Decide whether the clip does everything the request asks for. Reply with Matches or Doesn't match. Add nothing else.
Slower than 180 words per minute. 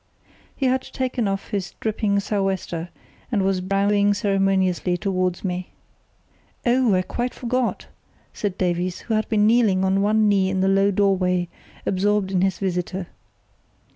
Matches